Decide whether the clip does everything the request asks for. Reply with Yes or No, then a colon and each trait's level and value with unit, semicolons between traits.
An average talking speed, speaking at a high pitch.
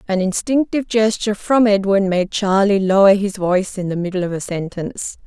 Yes: average, 180 wpm; high, 200 Hz